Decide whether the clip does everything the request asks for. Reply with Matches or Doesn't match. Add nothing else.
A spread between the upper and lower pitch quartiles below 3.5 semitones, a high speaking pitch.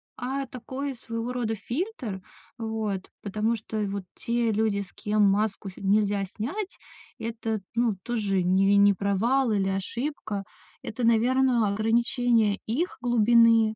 Matches